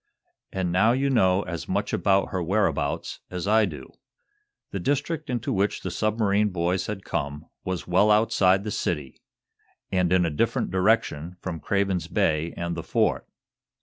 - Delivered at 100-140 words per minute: No, average, 165 wpm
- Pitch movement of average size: Yes, average, 3.4 semitones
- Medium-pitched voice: No, very low, 95 Hz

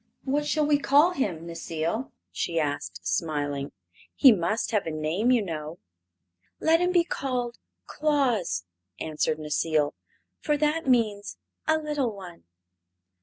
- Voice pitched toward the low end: No, high, 215 Hz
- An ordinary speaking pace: No, slow, 130 wpm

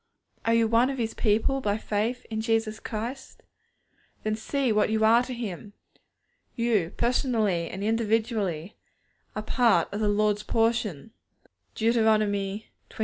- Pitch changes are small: Yes, narrow, 1.9 semitones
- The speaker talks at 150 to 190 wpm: No, average, 140 wpm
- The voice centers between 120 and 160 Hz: No, high, 220 Hz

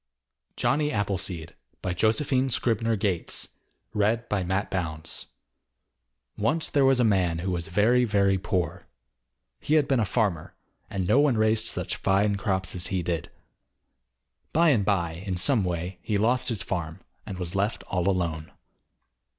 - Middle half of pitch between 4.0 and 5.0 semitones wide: Yes, average, 4.4 semitones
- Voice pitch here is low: Yes, low, 100 Hz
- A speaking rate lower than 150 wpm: Yes, average, 140 wpm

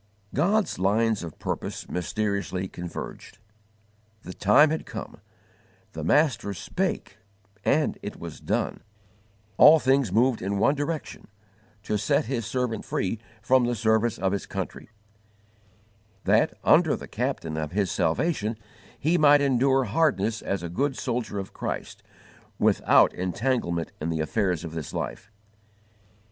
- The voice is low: Yes, low, 110 Hz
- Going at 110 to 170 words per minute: Yes, slow, 135 wpm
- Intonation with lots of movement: Yes, wide, 6.2 semitones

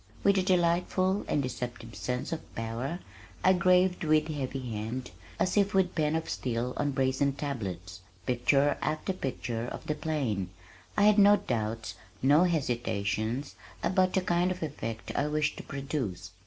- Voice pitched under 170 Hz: Yes, medium, 140 Hz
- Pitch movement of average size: No, wide, 6.8 semitones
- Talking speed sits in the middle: Yes, average, 155 wpm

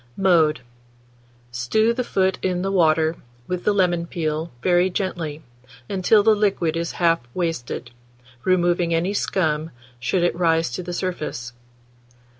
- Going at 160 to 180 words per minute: No, slow, 135 wpm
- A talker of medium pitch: Yes, medium, 175 Hz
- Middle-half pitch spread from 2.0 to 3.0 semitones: Yes, average, 2.7 semitones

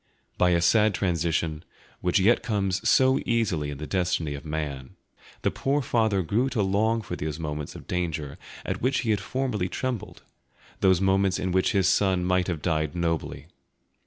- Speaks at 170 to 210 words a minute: Yes, average, 175 wpm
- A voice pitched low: Yes, very low, 90 Hz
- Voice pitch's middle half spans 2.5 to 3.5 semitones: No, average, 4.6 semitones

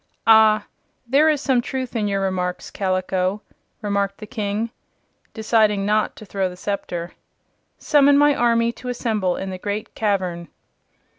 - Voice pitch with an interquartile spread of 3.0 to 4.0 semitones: Yes, average, 3.4 semitones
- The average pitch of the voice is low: No, high, 210 Hz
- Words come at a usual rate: Yes, average, 145 wpm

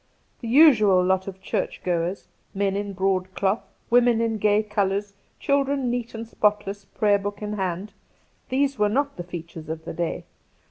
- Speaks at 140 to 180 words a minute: Yes, average, 170 wpm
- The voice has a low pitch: No, high, 205 Hz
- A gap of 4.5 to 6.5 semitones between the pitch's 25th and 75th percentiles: No, average, 3.4 semitones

